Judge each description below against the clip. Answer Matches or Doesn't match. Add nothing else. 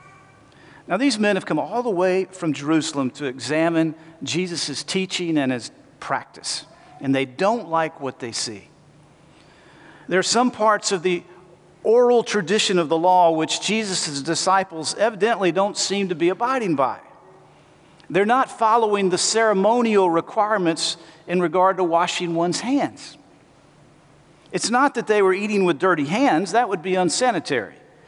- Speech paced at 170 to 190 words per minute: Doesn't match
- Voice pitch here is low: Doesn't match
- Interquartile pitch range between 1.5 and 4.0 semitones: Doesn't match